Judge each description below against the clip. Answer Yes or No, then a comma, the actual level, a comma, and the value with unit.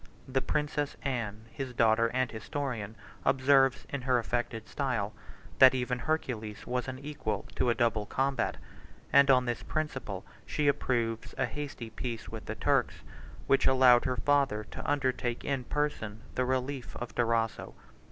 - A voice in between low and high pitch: No, low, 125 Hz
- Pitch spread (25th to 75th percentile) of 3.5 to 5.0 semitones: No, average, 3.0 semitones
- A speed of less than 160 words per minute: Yes, average, 150 wpm